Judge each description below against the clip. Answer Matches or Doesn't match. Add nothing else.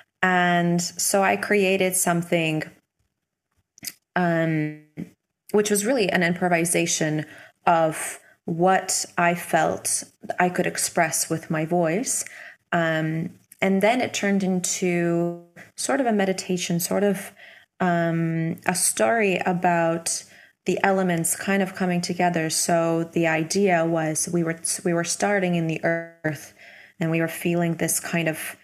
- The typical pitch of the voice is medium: Matches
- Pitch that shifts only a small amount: Matches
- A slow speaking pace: Matches